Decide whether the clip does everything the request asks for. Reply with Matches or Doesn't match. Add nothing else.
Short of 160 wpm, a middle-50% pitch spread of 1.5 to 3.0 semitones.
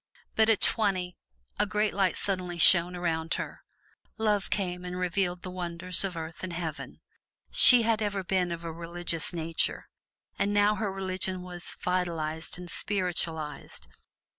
Matches